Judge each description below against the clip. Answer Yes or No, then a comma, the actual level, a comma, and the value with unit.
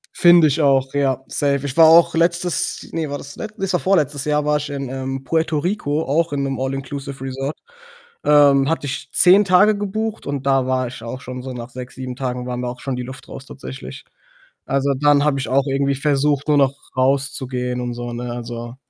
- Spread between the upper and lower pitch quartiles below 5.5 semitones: Yes, narrow, 2.4 semitones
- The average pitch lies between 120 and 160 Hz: Yes, medium, 140 Hz